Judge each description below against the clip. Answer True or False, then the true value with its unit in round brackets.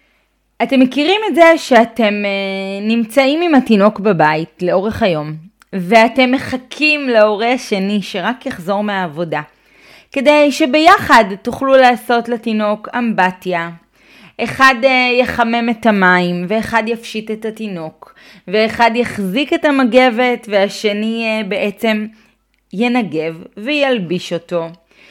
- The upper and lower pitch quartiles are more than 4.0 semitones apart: True (4.4 semitones)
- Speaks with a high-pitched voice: True (225 Hz)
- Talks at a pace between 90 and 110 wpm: True (100 wpm)